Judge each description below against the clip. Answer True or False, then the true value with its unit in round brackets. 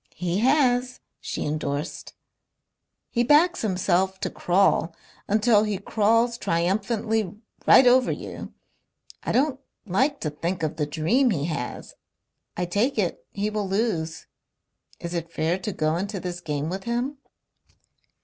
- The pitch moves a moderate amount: False (5.8 semitones)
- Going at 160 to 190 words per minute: False (140 wpm)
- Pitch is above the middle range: True (195 Hz)